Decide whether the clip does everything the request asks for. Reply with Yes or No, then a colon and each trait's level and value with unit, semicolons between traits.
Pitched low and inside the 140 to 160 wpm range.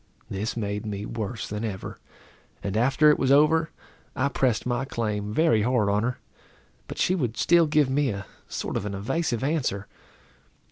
No: low, 120 Hz; average, 175 wpm